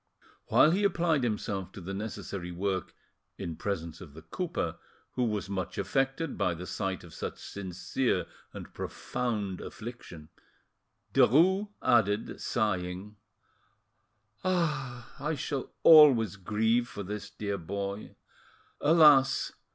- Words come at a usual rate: No, slow, 115 wpm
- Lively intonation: Yes, wide, 6.1 semitones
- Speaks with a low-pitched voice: Yes, low, 105 Hz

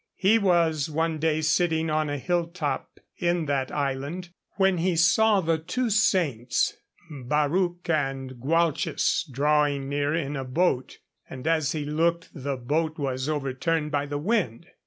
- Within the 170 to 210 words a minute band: No, average, 150 wpm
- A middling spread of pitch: Yes, average, 3.3 semitones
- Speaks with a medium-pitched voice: Yes, medium, 155 Hz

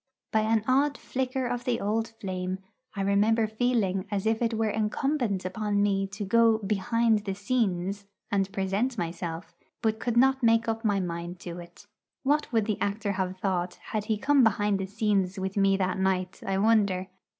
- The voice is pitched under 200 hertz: No, high, 205 Hz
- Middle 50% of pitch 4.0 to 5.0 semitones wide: No, average, 3.0 semitones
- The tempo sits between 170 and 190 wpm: Yes, average, 185 wpm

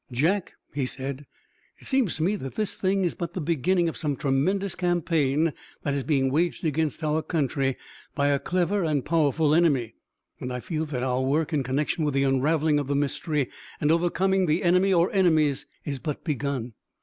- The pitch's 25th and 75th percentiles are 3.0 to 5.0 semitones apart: Yes, average, 3.9 semitones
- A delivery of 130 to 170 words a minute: No, average, 190 wpm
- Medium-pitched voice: Yes, medium, 155 Hz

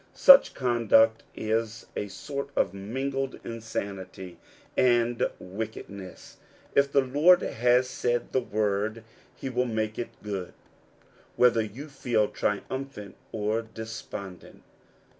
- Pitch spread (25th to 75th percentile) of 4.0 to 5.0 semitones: No, average, 3.4 semitones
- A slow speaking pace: Yes, slow, 110 wpm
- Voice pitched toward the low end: Yes, low, 115 Hz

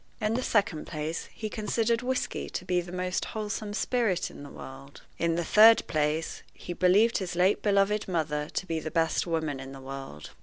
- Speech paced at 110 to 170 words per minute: No, average, 195 wpm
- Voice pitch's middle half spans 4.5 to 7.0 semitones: Yes, average, 5.3 semitones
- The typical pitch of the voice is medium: Yes, medium, 180 Hz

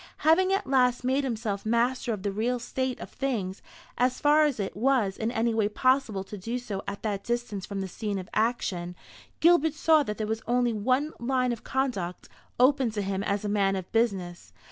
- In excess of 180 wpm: Yes, fast, 205 wpm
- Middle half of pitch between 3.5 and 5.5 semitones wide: Yes, average, 4.4 semitones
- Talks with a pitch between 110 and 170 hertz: No, high, 230 Hz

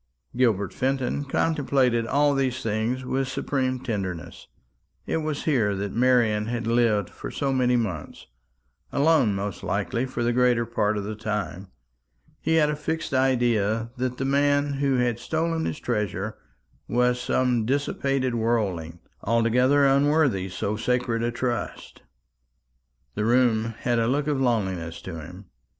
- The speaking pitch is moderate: No, low, 120 Hz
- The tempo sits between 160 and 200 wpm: No, average, 145 wpm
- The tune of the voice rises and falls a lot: No, average, 3.8 semitones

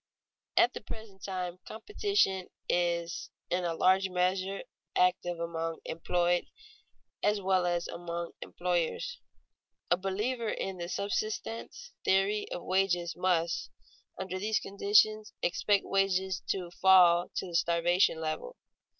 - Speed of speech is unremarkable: No, slow, 125 wpm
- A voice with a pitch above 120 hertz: Yes, medium, 185 Hz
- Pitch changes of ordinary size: No, narrow, 2.3 semitones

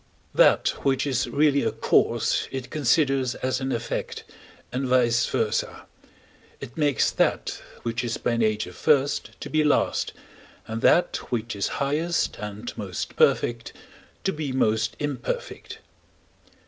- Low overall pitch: Yes, low, 130 Hz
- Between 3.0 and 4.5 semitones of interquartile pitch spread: Yes, average, 3.5 semitones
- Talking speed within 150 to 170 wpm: No, slow, 135 wpm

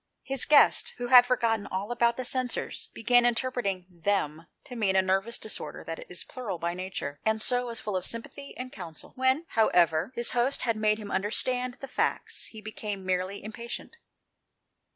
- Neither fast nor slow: Yes, average, 190 wpm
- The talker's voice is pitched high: Yes, high, 220 Hz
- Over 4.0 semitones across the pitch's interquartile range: Yes, average, 4.5 semitones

